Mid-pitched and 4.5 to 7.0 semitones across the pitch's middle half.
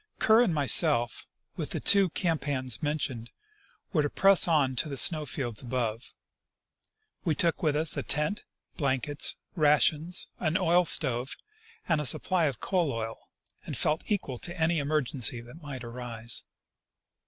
Yes: medium, 145 Hz; average, 4.8 semitones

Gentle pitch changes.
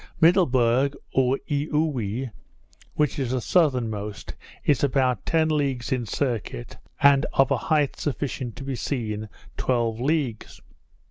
No: average, 3.6 semitones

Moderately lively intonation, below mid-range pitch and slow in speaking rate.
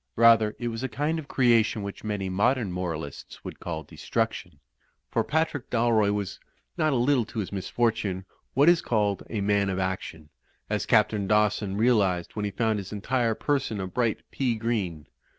No: average, 3.6 semitones; low, 105 Hz; average, 175 wpm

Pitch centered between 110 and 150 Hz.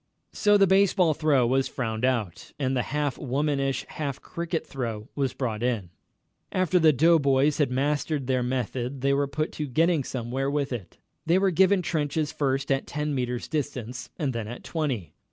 Yes: medium, 140 Hz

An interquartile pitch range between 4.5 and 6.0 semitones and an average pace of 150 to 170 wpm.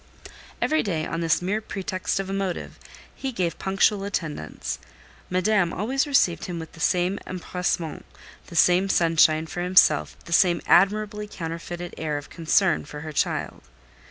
No: average, 3.0 semitones; average, 155 wpm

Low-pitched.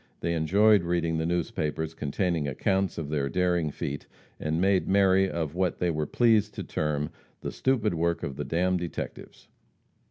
Yes: very low, 85 Hz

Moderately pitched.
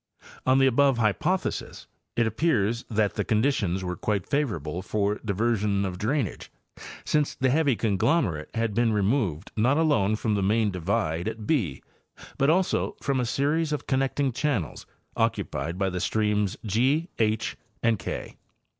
No: low, 110 Hz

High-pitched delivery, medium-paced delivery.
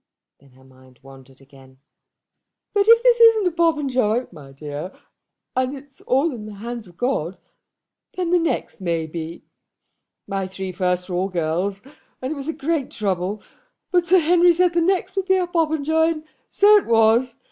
Yes: high, 245 Hz; average, 180 wpm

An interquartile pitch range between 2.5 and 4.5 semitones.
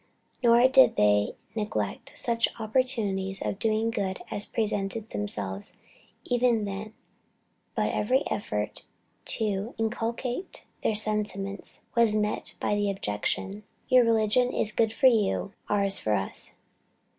Yes: average, 2.9 semitones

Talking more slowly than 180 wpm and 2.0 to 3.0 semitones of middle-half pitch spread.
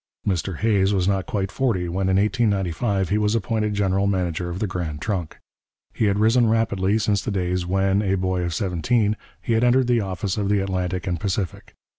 No: average, 200 wpm; narrow, 2.6 semitones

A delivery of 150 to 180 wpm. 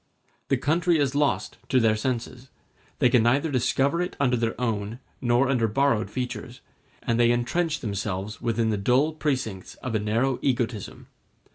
Yes: average, 160 wpm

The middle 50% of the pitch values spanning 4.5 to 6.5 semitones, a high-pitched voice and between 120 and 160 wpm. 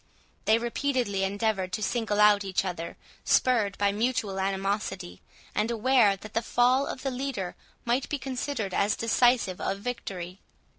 No: average, 4.0 semitones; high, 215 Hz; average, 150 wpm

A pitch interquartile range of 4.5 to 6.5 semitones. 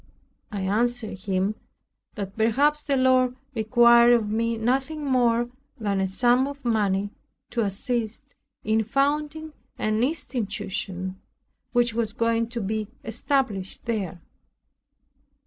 No: average, 3.4 semitones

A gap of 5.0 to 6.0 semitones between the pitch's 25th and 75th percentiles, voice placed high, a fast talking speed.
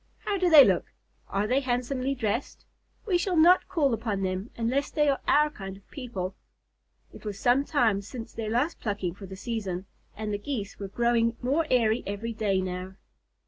No: wide, 5.5 semitones; high, 230 Hz; average, 185 wpm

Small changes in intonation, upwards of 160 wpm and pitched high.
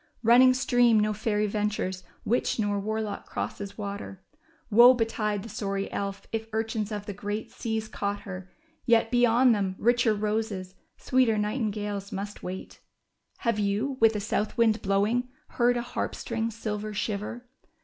No: narrow, 2.2 semitones; average, 150 wpm; high, 215 Hz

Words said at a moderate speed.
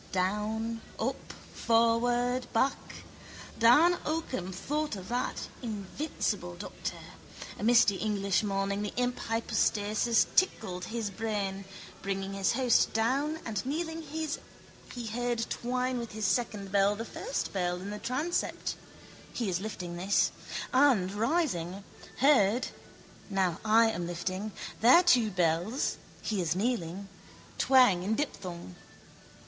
No: slow, 120 wpm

